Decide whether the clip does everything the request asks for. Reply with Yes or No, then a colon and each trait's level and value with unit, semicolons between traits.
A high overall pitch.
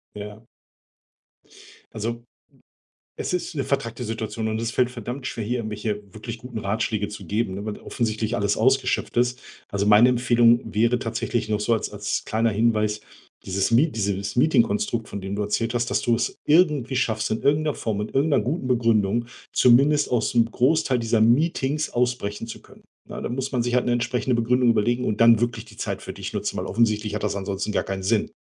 No: low, 115 Hz